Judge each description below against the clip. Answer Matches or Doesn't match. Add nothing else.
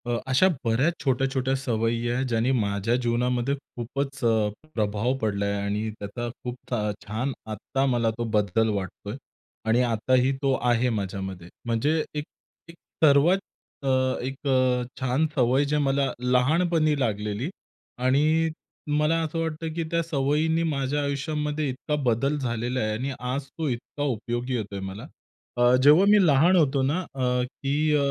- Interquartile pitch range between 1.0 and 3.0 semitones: Doesn't match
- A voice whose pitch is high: Doesn't match